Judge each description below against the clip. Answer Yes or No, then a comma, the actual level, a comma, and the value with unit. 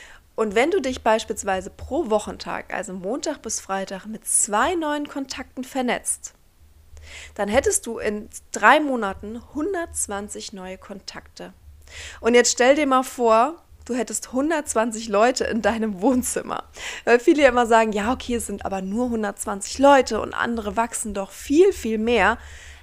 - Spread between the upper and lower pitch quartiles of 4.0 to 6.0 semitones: Yes, average, 4.7 semitones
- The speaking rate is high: No, average, 150 wpm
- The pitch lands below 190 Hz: No, high, 225 Hz